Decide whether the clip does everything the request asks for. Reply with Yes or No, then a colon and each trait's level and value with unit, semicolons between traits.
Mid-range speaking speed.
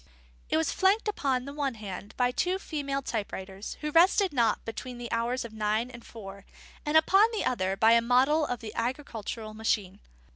Yes: average, 195 wpm